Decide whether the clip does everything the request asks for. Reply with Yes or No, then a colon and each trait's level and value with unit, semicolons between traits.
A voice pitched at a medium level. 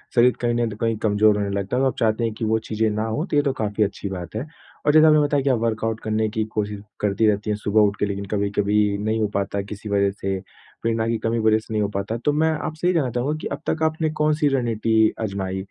No: low, 110 Hz